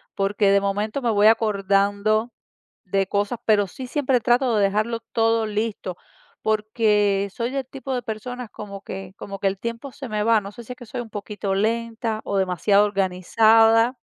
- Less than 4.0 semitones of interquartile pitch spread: Yes, narrow, 2.6 semitones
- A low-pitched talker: No, high, 215 Hz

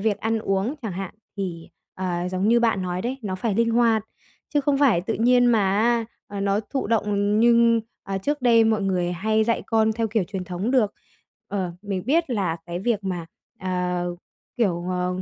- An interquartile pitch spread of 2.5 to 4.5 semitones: Yes, average, 3.9 semitones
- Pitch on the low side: No, high, 210 Hz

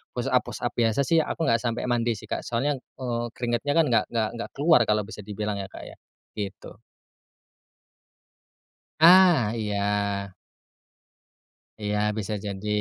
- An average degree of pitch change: Yes, average, 3.8 semitones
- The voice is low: Yes, low, 115 Hz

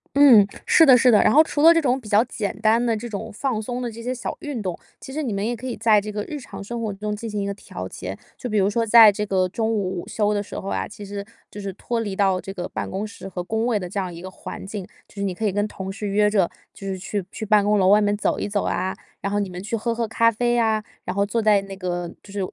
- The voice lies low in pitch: No, high, 210 Hz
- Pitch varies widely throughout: No, average, 2.7 semitones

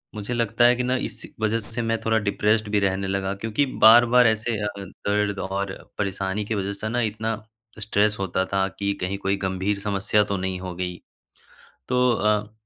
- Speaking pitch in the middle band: No, low, 105 Hz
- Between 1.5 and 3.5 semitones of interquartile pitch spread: Yes, narrow, 2.4 semitones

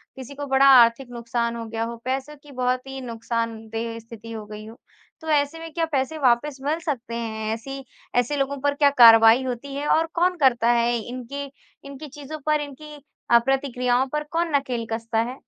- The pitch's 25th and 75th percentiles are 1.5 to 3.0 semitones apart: No, average, 3.6 semitones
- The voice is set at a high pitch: Yes, very high, 255 Hz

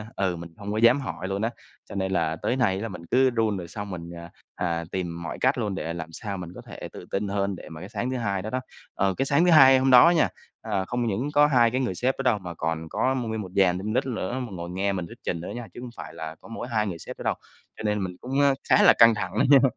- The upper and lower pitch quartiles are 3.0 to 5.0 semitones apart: No, wide, 5.5 semitones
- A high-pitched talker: No, low, 100 Hz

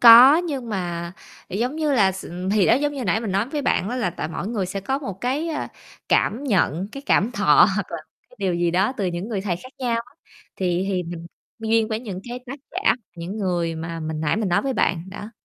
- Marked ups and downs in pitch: Yes, wide, 5.7 semitones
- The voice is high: Yes, high, 200 Hz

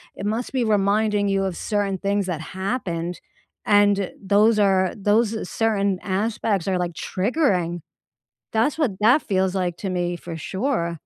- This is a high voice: Yes, high, 200 Hz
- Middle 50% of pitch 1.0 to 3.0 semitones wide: Yes, average, 2.7 semitones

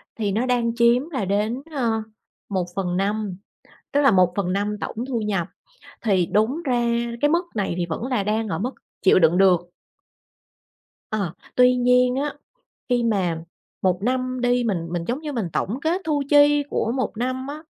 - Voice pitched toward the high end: Yes, high, 230 Hz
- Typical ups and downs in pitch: Yes, average, 4.6 semitones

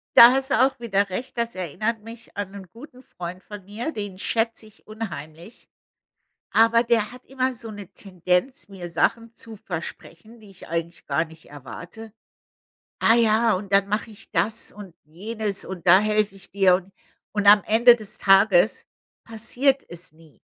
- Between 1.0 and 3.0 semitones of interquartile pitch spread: No, average, 3.8 semitones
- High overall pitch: Yes, high, 210 Hz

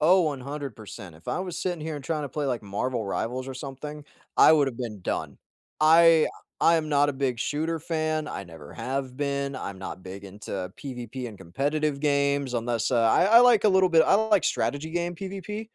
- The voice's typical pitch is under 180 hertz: Yes, medium, 140 Hz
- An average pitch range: Yes, average, 4.9 semitones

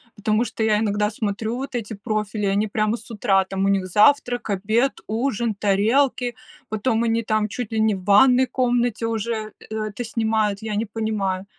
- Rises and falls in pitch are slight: Yes, narrow, 2.2 semitones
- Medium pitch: No, high, 220 Hz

